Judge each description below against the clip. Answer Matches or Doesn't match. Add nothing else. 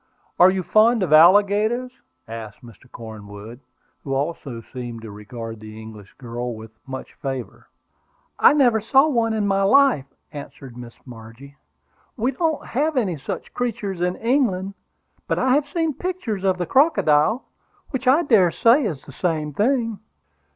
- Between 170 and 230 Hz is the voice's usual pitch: Matches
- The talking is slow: Doesn't match